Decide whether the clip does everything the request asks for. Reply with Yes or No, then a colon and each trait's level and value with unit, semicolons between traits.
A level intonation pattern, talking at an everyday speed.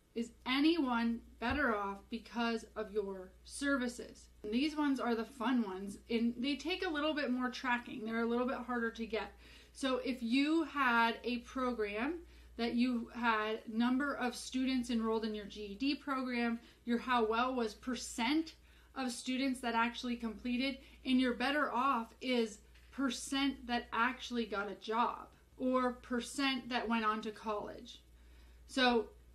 Yes: narrow, 2.3 semitones; average, 155 wpm